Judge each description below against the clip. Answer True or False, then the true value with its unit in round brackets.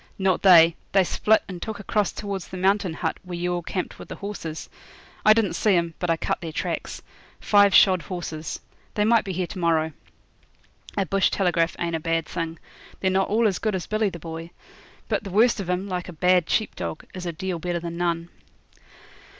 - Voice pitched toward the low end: False (180 Hz)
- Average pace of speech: False (210 wpm)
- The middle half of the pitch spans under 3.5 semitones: True (2.8 semitones)